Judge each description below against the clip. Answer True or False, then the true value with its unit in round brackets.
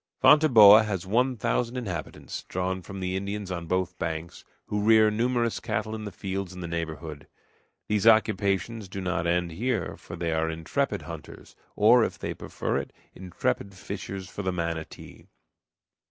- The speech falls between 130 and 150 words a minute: False (160 wpm)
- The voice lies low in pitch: True (95 Hz)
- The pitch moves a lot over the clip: False (3.8 semitones)